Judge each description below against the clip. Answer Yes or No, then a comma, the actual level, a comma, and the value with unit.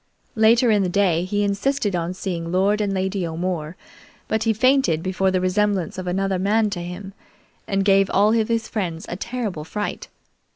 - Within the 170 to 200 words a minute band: Yes, average, 180 wpm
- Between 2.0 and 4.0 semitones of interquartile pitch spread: Yes, average, 2.8 semitones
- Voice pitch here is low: No, high, 195 Hz